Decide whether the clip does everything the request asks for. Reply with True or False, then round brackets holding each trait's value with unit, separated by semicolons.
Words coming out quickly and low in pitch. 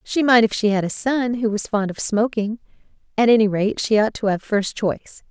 False (240 wpm; 220 Hz)